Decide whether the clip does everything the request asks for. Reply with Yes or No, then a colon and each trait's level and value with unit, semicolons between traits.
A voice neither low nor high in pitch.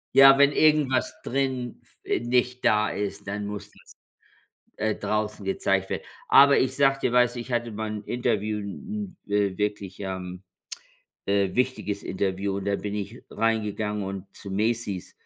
No: low, 105 Hz